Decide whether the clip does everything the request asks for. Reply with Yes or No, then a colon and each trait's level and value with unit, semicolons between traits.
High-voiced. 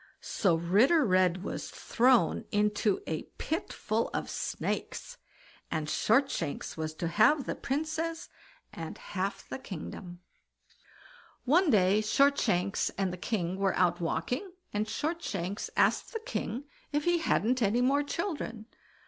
Yes: high, 215 Hz